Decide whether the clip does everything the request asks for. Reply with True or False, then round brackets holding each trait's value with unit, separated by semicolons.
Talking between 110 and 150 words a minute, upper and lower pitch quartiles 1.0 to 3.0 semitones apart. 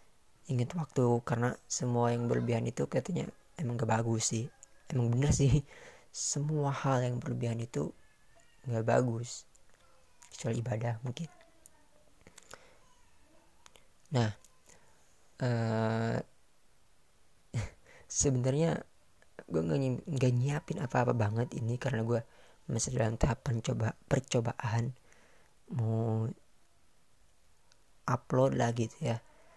False (95 wpm; 2.6 semitones)